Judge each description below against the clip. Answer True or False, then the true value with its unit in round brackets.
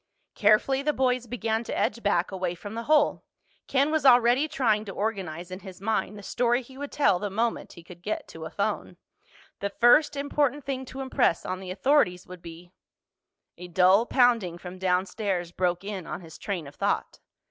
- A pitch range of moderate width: False (5.7 semitones)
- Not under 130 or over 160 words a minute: False (190 wpm)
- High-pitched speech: True (210 Hz)